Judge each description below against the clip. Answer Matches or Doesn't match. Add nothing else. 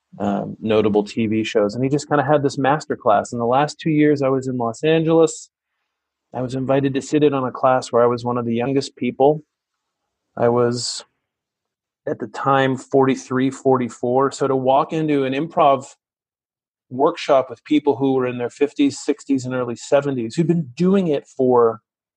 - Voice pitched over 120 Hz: Matches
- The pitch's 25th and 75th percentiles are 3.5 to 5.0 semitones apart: Doesn't match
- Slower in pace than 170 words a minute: Doesn't match